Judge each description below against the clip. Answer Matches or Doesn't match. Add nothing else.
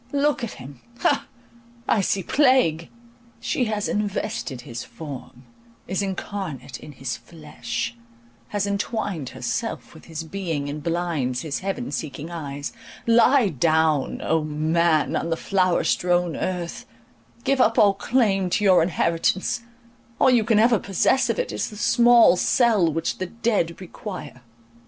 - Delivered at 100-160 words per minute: Matches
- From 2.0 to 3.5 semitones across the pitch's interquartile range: Doesn't match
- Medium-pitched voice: Matches